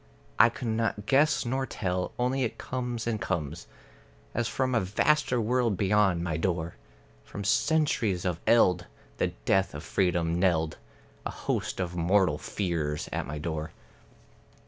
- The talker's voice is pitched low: Yes, very low, 95 Hz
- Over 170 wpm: No, average, 145 wpm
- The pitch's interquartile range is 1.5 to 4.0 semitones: No, wide, 5.6 semitones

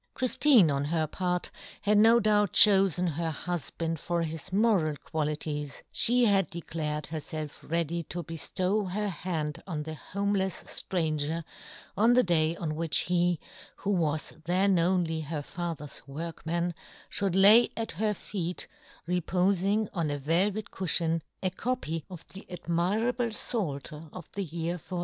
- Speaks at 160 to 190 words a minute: No, average, 145 wpm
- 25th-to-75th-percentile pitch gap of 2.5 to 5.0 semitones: Yes, average, 3.7 semitones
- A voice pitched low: No, medium, 175 Hz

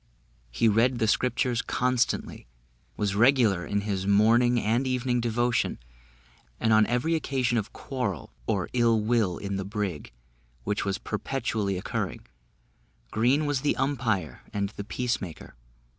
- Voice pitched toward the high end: No, low, 115 Hz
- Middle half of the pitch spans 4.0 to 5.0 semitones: No, average, 3.6 semitones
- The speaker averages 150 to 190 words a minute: No, average, 140 wpm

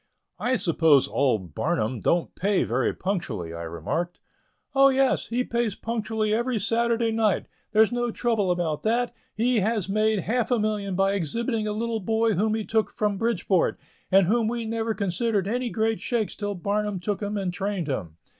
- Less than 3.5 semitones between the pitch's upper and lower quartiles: No, average, 4.1 semitones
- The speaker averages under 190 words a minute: Yes, average, 175 wpm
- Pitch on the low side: No, high, 210 Hz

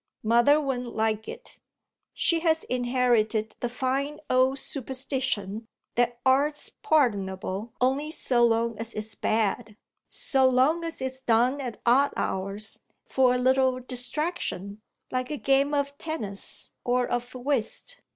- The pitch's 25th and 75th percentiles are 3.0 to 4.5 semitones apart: Yes, average, 3.3 semitones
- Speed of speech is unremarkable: No, slow, 130 wpm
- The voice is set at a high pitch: Yes, very high, 250 Hz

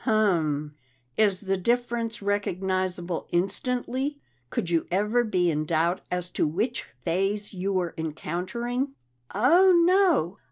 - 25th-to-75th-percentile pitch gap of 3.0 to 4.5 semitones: No, wide, 5.4 semitones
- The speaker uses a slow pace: Yes, slow, 120 wpm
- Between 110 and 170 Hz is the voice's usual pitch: No, high, 195 Hz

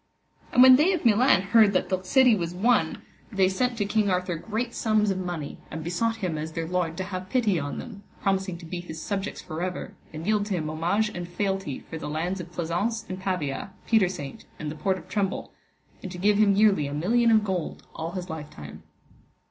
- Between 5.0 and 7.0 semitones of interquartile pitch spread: No, average, 3.9 semitones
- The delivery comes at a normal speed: No, fast, 215 wpm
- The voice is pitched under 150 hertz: No, medium, 185 Hz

